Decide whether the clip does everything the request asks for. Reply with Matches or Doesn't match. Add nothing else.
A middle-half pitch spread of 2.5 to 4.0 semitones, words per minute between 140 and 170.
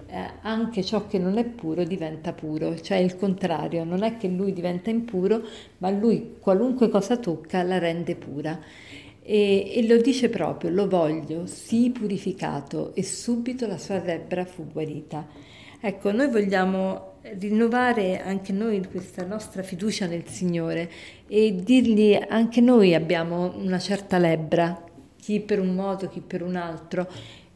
Matches